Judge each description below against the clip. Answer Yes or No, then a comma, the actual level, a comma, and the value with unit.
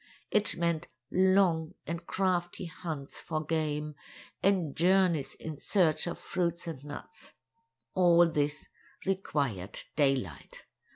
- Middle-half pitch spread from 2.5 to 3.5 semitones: Yes, average, 3.2 semitones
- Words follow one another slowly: Yes, slow, 110 wpm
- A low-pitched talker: No, medium, 165 Hz